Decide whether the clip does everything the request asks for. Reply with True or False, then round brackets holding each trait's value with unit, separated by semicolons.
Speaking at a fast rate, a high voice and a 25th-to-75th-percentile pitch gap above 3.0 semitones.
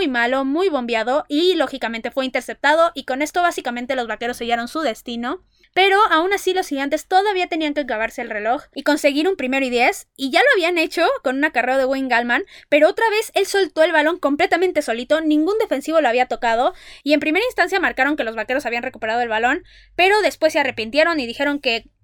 True (210 wpm; 295 Hz; 5.6 semitones)